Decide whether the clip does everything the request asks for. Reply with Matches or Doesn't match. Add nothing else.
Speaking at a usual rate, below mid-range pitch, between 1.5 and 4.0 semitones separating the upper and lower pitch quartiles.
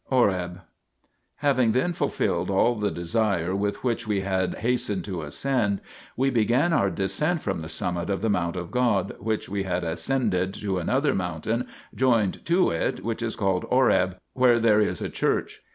Doesn't match